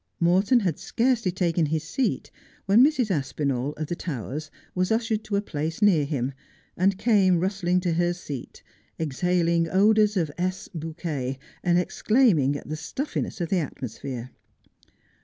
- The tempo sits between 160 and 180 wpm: No, average, 150 wpm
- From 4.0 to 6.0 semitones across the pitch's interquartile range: Yes, average, 4.7 semitones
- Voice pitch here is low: No, medium, 175 Hz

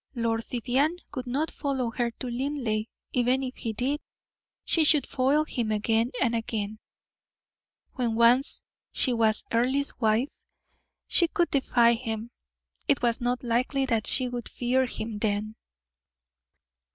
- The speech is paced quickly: No, average, 140 wpm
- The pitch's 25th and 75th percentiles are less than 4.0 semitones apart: Yes, average, 2.7 semitones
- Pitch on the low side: No, high, 245 Hz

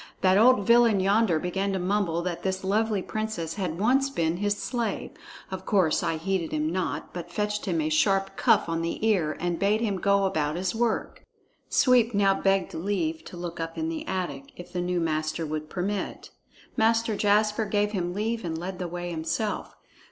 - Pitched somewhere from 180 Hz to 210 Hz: Yes, high, 190 Hz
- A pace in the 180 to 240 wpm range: Yes, average, 190 wpm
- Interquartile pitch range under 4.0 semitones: Yes, average, 3.6 semitones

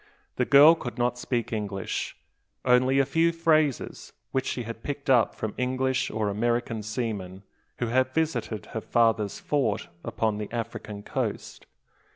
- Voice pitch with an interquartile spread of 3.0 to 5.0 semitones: Yes, average, 3.3 semitones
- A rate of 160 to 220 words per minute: No, average, 150 wpm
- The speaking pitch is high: No, low, 120 Hz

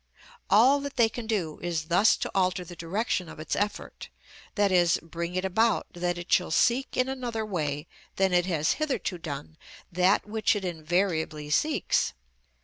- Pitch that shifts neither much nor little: Yes, average, 4.8 semitones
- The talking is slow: No, average, 165 wpm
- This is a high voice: No, medium, 180 Hz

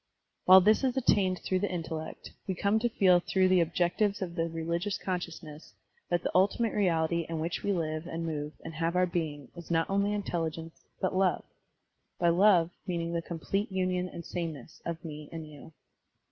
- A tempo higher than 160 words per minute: Yes, average, 190 wpm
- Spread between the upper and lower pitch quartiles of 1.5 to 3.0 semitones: Yes, narrow, 2.5 semitones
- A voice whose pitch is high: No, medium, 175 Hz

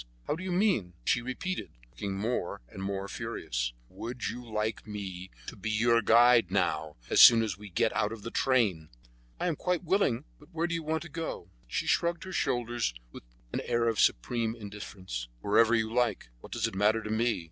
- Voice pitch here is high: No, low, 115 Hz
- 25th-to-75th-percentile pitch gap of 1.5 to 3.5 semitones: No, average, 4.1 semitones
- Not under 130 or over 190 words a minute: No, average, 200 wpm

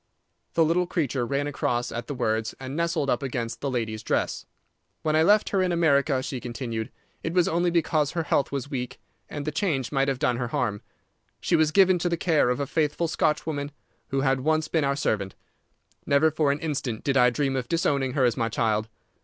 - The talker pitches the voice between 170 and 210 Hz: No, medium, 140 Hz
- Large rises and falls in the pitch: No, average, 4.2 semitones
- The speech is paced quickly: Yes, fast, 215 wpm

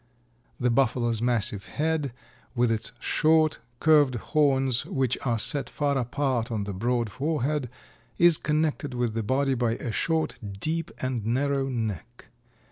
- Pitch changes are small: No, average, 3.8 semitones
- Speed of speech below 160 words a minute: Yes, average, 140 wpm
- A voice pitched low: Yes, low, 130 Hz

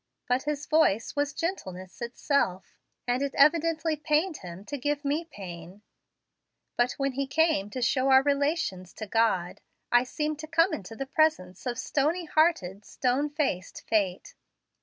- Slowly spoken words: No, average, 155 wpm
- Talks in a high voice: Yes, very high, 275 Hz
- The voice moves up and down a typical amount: No, wide, 6.5 semitones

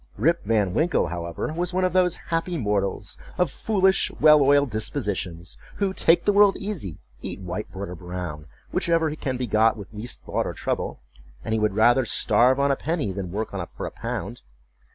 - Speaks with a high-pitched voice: No, low, 120 Hz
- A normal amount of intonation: No, wide, 9.0 semitones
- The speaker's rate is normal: Yes, average, 185 wpm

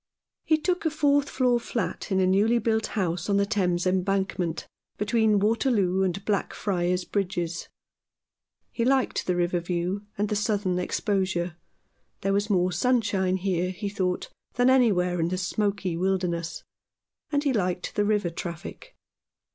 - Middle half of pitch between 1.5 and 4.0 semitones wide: Yes, average, 3.2 semitones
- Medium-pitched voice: No, high, 195 Hz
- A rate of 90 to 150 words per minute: Yes, average, 145 wpm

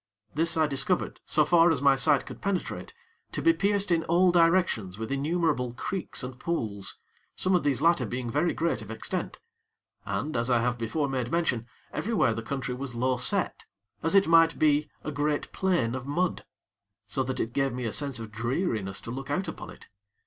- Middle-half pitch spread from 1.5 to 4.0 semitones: No, wide, 5.4 semitones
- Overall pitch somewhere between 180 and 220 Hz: No, medium, 140 Hz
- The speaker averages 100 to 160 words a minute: No, average, 195 wpm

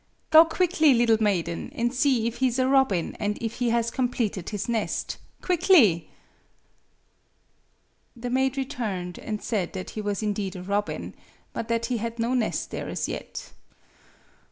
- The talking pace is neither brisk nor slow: Yes, average, 160 wpm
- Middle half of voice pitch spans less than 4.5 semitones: Yes, average, 3.7 semitones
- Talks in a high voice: Yes, high, 230 Hz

